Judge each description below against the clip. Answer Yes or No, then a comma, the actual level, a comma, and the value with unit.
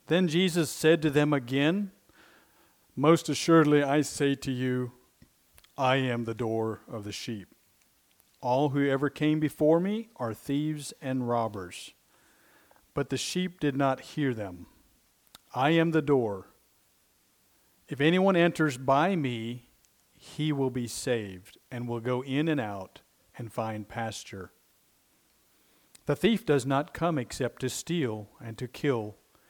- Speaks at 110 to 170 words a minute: Yes, average, 140 wpm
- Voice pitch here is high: No, low, 135 Hz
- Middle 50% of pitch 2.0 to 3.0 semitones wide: No, average, 4.4 semitones